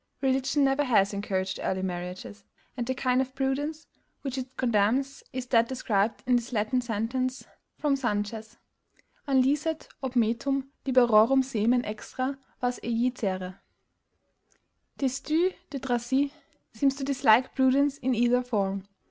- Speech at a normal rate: No, slow, 130 wpm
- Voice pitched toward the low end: No, very high, 250 Hz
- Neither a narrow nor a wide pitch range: Yes, average, 3.6 semitones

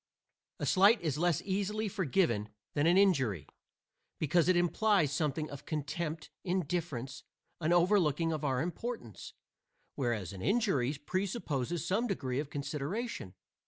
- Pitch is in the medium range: Yes, medium, 165 Hz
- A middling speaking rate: No, slow, 125 wpm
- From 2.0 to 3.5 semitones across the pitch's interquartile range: No, wide, 5.4 semitones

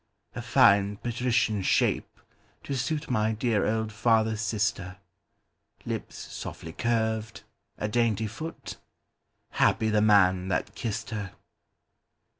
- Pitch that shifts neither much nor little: No, narrow, 2.2 semitones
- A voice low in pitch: Yes, low, 110 Hz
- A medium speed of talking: No, slow, 95 wpm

